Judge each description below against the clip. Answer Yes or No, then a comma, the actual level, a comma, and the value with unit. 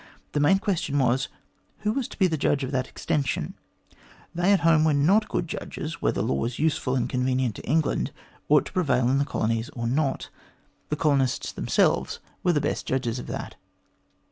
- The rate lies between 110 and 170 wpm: No, average, 185 wpm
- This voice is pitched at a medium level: Yes, medium, 145 Hz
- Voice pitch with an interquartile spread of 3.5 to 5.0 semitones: Yes, average, 4.4 semitones